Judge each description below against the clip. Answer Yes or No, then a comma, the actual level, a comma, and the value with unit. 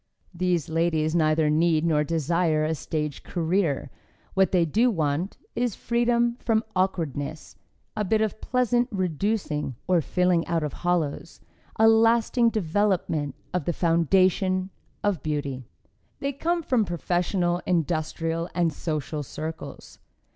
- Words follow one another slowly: Yes, slow, 125 wpm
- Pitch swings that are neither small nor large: Yes, average, 4.6 semitones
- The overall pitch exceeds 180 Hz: No, medium, 175 Hz